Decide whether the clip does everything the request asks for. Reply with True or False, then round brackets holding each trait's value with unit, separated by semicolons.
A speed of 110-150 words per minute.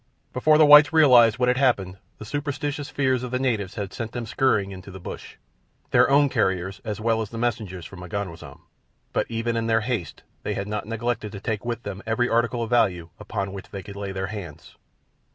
False (205 wpm)